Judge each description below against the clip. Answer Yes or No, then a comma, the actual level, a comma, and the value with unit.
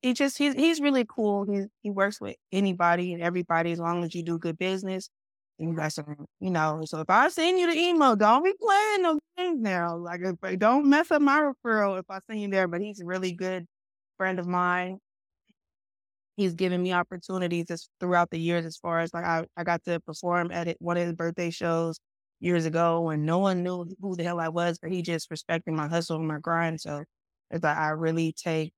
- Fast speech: Yes, fast, 225 wpm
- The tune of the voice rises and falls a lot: No, average, 3.0 semitones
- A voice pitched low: No, medium, 175 Hz